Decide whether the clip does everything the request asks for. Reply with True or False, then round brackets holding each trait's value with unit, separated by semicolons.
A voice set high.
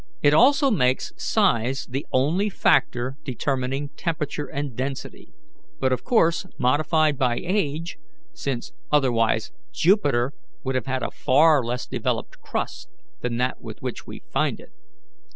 False (140 Hz)